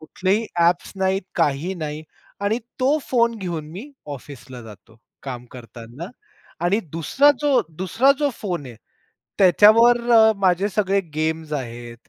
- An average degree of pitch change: No, wide, 6.8 semitones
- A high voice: No, medium, 175 Hz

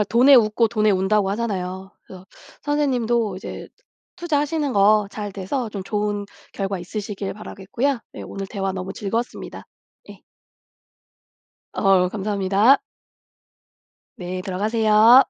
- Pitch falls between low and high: No, high, 210 Hz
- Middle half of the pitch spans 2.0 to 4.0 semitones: Yes, average, 3.3 semitones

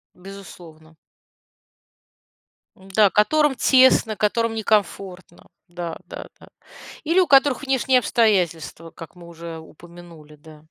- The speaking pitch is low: No, high, 190 Hz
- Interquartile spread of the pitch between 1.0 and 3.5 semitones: No, wide, 5.6 semitones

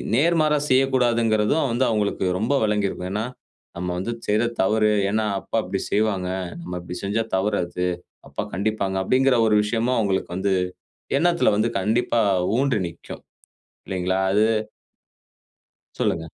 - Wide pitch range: No, average, 3.7 semitones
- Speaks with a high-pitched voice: No, low, 105 Hz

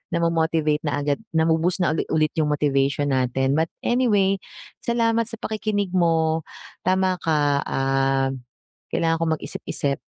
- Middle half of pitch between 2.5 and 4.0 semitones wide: No, average, 4.5 semitones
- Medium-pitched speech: Yes, medium, 160 Hz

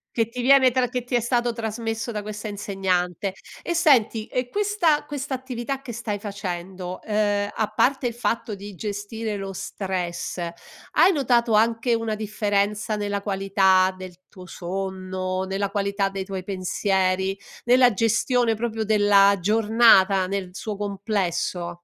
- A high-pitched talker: Yes, high, 205 Hz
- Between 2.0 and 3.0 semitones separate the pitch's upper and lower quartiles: No, average, 3.4 semitones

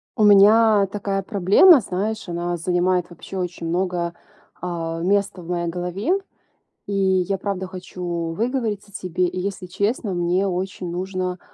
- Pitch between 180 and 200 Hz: Yes, medium, 185 Hz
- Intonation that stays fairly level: Yes, narrow, 2.2 semitones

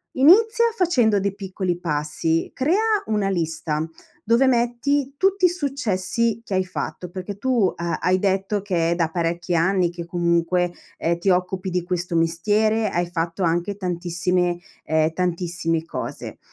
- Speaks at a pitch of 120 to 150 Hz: No, medium, 185 Hz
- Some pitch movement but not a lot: Yes, average, 4.3 semitones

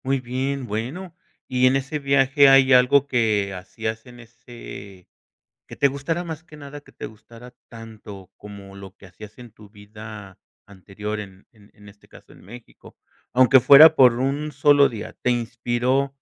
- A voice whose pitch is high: No, low, 120 Hz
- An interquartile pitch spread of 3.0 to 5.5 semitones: Yes, average, 4.6 semitones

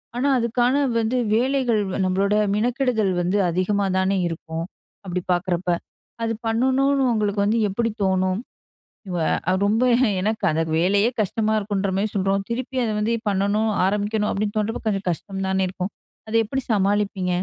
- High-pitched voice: Yes, high, 205 Hz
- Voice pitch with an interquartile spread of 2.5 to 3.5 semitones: Yes, average, 3.0 semitones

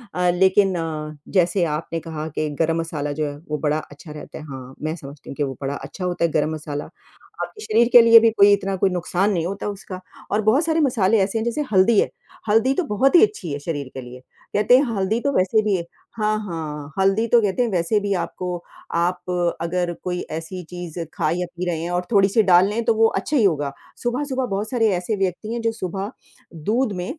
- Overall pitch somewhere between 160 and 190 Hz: Yes, medium, 185 Hz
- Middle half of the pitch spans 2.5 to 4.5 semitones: No, average, 5.0 semitones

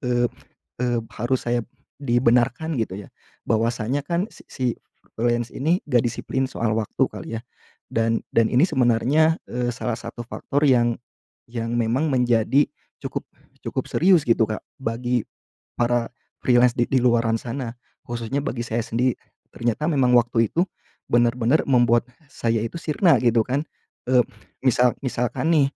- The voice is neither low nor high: No, low, 120 Hz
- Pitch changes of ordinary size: No, narrow, 2.3 semitones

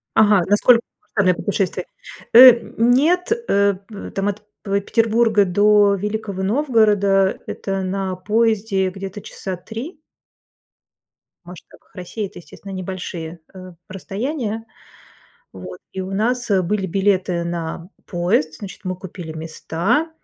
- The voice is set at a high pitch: Yes, high, 195 Hz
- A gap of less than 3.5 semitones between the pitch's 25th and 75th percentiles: Yes, average, 3.1 semitones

